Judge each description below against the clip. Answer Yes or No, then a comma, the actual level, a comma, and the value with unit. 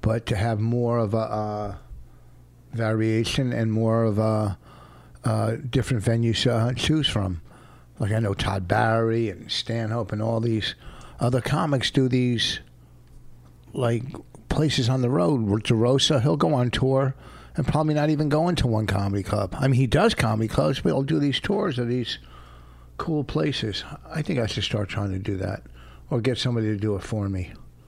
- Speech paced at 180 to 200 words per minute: Yes, average, 185 wpm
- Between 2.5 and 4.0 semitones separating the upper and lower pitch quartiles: No, average, 4.4 semitones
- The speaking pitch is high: No, low, 115 Hz